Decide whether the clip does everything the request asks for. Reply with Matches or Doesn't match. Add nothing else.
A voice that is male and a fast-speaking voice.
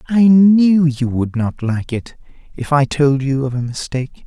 Doesn't match